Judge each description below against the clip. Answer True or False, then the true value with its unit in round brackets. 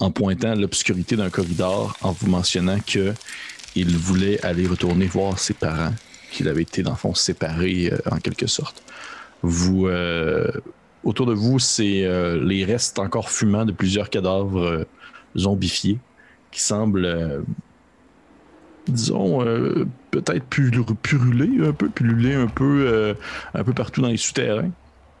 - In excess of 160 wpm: False (150 wpm)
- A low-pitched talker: True (95 Hz)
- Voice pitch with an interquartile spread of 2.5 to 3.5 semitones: False (4.0 semitones)